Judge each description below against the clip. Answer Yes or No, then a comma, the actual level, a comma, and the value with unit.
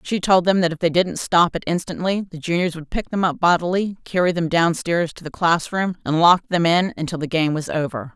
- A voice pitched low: No, medium, 170 Hz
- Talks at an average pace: No, fast, 235 wpm